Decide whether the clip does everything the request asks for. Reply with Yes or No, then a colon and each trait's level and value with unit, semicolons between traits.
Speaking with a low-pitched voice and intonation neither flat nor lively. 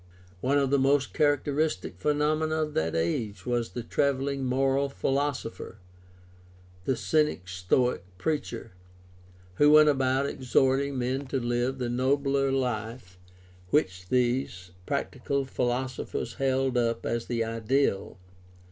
Yes: low, 130 Hz; average, 3.0 semitones